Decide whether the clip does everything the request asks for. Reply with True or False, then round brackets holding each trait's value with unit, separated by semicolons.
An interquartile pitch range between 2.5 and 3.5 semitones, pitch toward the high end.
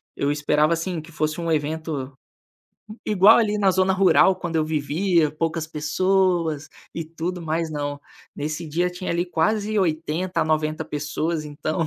False (2.9 semitones; 165 Hz)